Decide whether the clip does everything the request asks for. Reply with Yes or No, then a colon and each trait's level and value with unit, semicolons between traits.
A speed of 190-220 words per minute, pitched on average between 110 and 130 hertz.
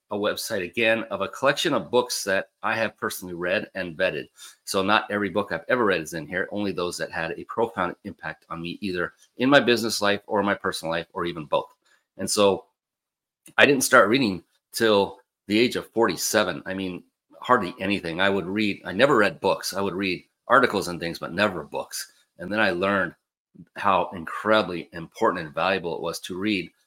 No: average, 200 wpm; low, 100 Hz